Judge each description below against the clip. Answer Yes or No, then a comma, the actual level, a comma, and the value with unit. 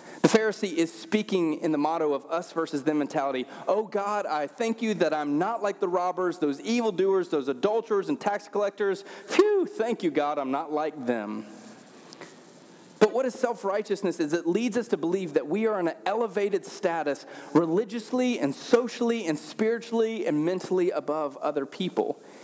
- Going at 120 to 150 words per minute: No, average, 175 wpm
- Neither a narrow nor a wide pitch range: No, wide, 6.4 semitones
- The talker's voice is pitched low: No, high, 190 Hz